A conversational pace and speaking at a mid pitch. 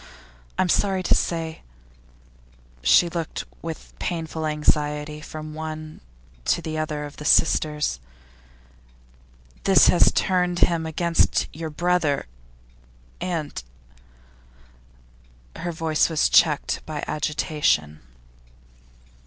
No: slow, 105 wpm; medium, 155 Hz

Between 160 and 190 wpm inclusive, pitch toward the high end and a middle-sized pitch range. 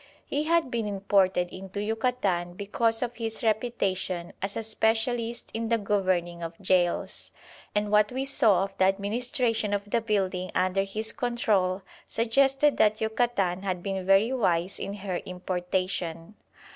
No: average, 145 wpm; high, 205 Hz; average, 3.5 semitones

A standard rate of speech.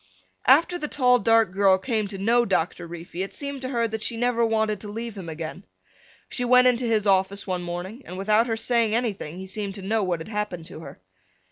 No: fast, 225 wpm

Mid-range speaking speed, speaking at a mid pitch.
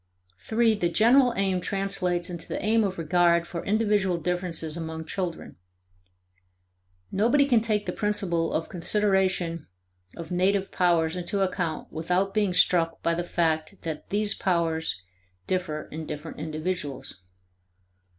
No: slow, 130 wpm; medium, 180 Hz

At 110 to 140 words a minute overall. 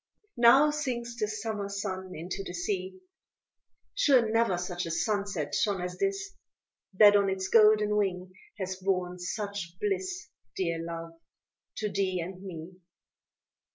Yes: slow, 135 wpm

